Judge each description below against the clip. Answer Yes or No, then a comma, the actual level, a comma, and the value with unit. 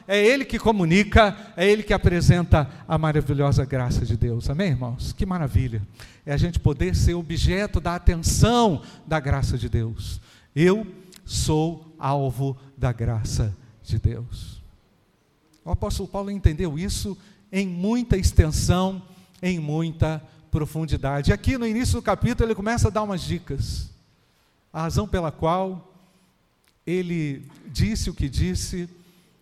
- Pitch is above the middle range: No, medium, 155 Hz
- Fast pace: No, average, 140 wpm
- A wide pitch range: Yes, wide, 7.7 semitones